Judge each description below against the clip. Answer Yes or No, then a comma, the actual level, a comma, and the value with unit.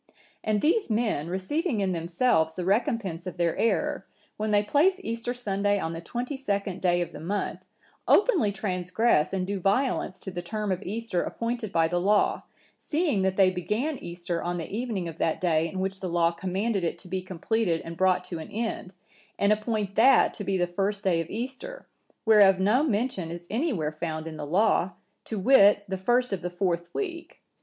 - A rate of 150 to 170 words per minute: No, average, 200 wpm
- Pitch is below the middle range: No, high, 195 Hz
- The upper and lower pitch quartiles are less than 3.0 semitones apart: No, average, 4.5 semitones